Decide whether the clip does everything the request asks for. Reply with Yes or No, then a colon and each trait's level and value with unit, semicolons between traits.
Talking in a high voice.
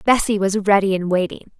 Yes: high, 200 Hz